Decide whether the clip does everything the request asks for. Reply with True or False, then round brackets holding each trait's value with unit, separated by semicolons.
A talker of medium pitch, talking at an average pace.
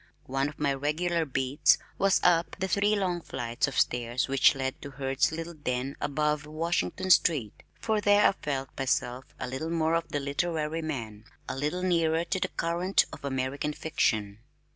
True (150 Hz; 170 wpm)